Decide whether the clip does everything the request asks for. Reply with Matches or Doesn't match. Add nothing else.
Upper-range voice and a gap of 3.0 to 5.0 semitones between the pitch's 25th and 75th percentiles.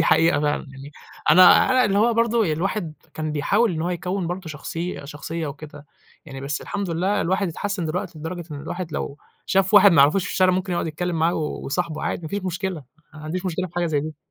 Doesn't match